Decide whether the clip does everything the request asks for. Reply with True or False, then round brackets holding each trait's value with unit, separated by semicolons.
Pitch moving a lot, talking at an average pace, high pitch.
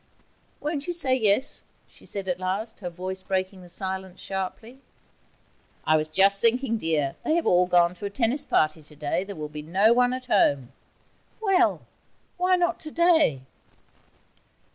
True (6.5 semitones; 155 wpm; 195 Hz)